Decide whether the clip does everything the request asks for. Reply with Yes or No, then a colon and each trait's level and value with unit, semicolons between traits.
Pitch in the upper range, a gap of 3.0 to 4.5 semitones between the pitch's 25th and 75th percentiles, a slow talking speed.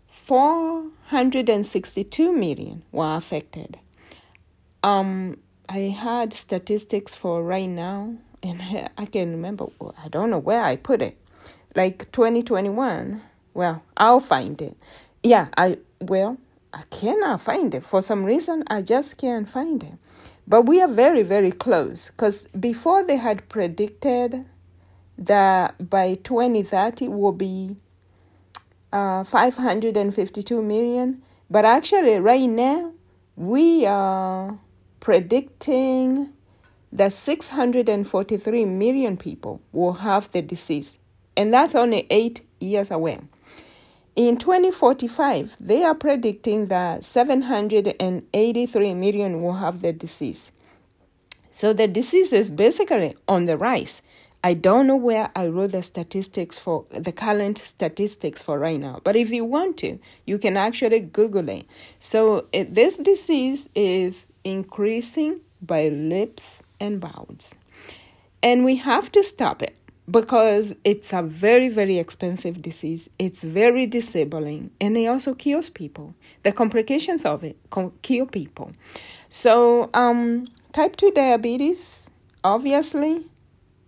No: high, 210 Hz; average, 5.2 semitones; slow, 125 wpm